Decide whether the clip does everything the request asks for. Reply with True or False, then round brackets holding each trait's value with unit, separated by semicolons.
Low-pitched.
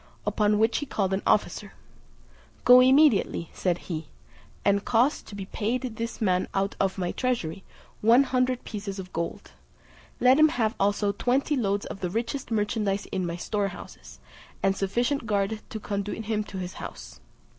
False (210 Hz)